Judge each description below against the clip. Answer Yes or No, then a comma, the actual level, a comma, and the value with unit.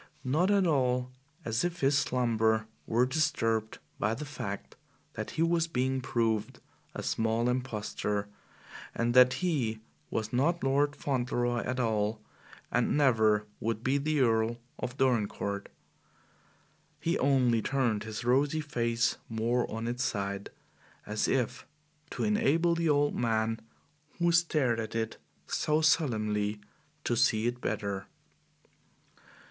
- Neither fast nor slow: No, slow, 130 wpm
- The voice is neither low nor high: No, low, 120 Hz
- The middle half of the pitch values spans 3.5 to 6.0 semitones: Yes, average, 4.2 semitones